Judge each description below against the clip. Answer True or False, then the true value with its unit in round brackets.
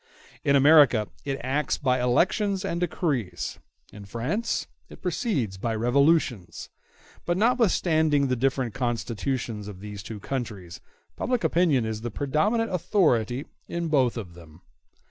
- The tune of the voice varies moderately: False (6.8 semitones)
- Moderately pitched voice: False (130 Hz)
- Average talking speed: False (130 wpm)